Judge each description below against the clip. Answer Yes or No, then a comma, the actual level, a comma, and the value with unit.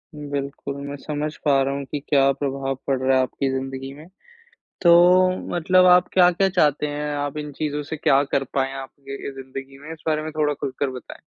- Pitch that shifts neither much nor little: No, narrow, 2.0 semitones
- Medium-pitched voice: Yes, medium, 145 Hz